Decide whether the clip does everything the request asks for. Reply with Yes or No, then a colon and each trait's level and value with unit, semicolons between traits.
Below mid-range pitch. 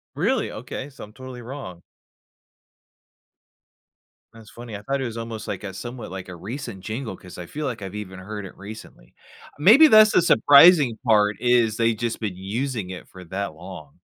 Yes: low, 110 Hz